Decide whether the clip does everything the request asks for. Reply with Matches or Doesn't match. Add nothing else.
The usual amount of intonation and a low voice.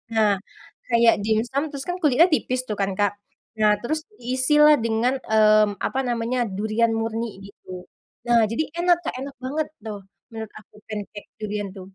Doesn't match